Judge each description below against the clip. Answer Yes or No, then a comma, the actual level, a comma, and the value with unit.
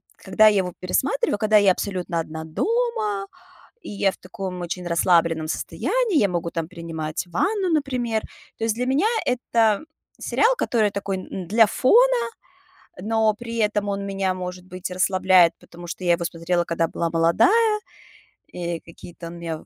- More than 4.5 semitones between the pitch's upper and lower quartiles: Yes, average, 4.9 semitones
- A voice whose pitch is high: Yes, high, 195 Hz